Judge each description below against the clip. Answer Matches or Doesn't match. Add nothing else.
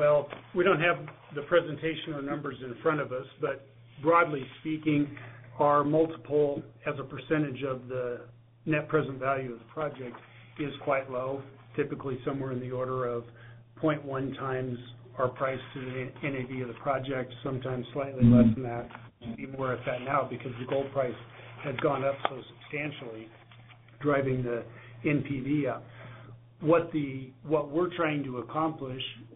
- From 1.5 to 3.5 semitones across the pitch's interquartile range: Matches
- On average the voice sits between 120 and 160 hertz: Matches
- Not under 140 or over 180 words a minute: Matches